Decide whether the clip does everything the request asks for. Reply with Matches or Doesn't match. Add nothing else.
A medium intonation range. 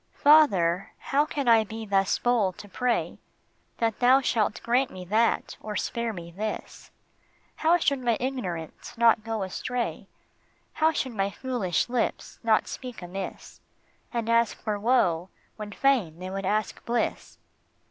Matches